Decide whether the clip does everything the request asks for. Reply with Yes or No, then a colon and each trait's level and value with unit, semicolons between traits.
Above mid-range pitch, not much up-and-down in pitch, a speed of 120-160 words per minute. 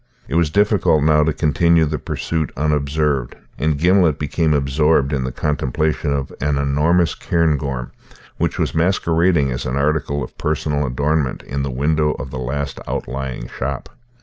No: very low, 75 Hz; narrow, 2.3 semitones; average, 155 wpm